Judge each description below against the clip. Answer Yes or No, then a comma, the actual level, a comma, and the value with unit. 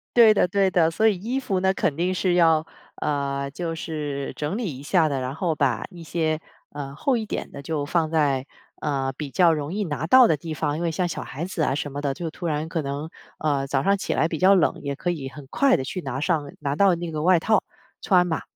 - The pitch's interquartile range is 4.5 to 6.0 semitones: No, average, 4.0 semitones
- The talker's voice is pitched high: No, medium, 160 Hz